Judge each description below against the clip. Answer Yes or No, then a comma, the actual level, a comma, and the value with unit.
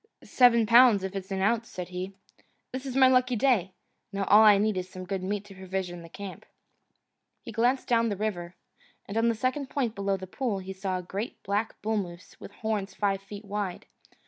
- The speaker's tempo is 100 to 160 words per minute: No, fast, 205 wpm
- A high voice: Yes, high, 200 Hz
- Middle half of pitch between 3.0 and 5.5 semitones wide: Yes, average, 3.3 semitones